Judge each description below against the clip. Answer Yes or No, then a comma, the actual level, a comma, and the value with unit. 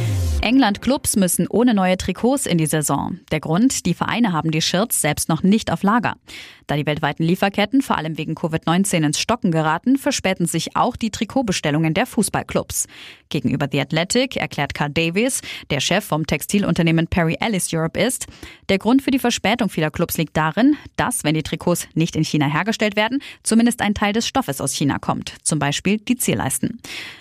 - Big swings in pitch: Yes, wide, 6.3 semitones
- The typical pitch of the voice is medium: Yes, medium, 175 Hz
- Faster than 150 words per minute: Yes, average, 185 wpm